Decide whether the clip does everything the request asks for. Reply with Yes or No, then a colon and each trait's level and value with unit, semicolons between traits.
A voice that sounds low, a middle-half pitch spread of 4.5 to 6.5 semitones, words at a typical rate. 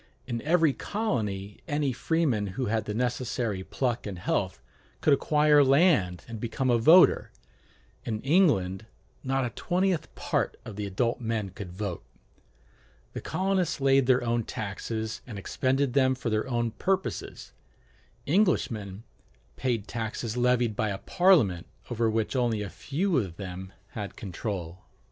Yes: low, 120 Hz; average, 5.1 semitones; average, 145 wpm